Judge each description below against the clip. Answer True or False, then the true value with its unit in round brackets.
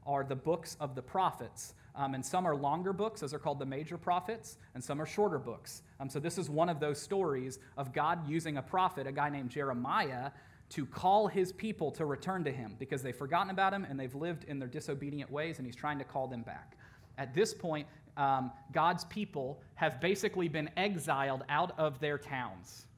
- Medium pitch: True (145 Hz)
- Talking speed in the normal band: False (210 wpm)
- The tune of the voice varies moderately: True (4.1 semitones)